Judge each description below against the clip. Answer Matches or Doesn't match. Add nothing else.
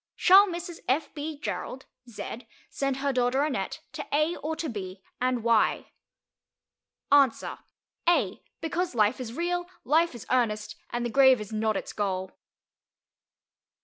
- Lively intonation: Matches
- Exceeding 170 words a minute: Doesn't match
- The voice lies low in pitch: Doesn't match